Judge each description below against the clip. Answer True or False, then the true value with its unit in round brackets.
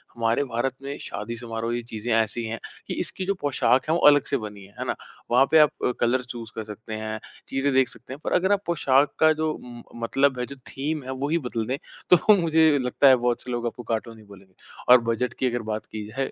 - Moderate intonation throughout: True (3.7 semitones)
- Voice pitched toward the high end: False (125 Hz)